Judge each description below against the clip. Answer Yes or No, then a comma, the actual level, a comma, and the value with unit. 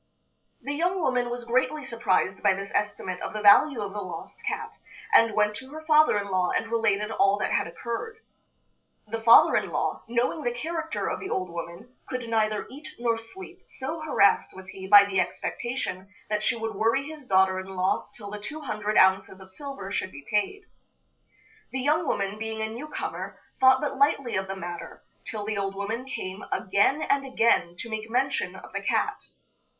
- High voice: Yes, high, 225 Hz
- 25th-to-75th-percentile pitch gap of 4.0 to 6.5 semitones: Yes, average, 5.1 semitones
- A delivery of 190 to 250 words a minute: Yes, average, 195 wpm